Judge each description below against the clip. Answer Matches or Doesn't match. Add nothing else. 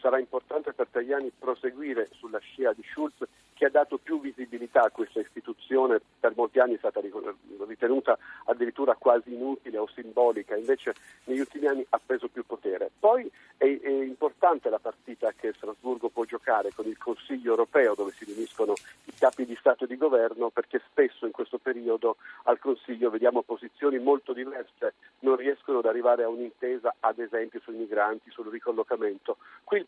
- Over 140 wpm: Matches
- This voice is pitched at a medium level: Matches